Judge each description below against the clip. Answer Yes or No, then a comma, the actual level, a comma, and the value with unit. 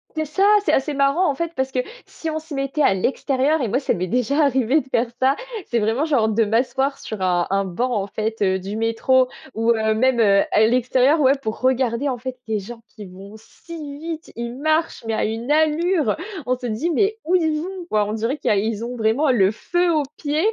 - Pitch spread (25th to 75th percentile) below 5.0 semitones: No, average, 5.3 semitones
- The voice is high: Yes, very high, 255 Hz